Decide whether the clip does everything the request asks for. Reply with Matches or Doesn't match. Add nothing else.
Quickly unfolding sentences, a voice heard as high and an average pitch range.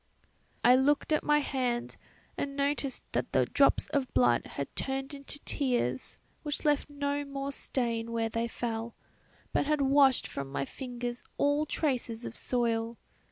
Doesn't match